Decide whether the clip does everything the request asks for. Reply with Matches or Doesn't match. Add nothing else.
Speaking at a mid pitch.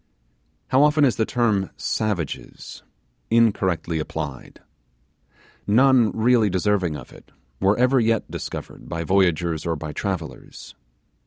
Doesn't match